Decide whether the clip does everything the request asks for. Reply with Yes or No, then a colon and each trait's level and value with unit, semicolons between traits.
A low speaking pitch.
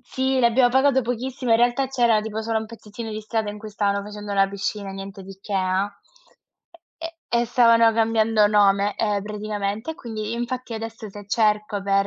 No: high, 220 Hz